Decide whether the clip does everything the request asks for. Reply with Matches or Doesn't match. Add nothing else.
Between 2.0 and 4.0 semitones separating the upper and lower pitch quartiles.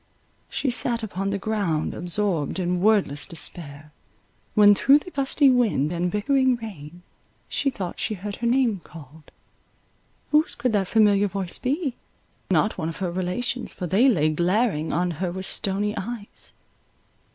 Doesn't match